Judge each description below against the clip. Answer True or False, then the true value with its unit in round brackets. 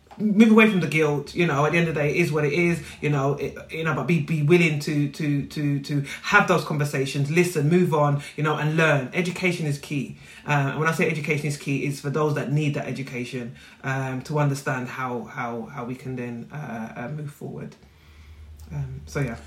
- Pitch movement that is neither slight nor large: True (3.5 semitones)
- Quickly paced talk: True (230 wpm)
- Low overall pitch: False (145 Hz)